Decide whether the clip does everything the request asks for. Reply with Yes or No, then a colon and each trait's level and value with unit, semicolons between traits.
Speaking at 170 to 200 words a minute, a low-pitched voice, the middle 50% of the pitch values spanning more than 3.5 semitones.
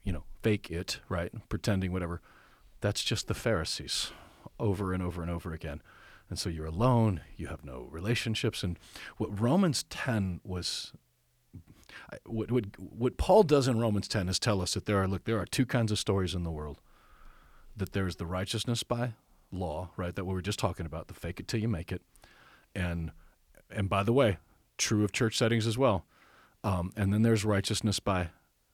Yes: average, 190 wpm; low, 100 Hz; average, 4.3 semitones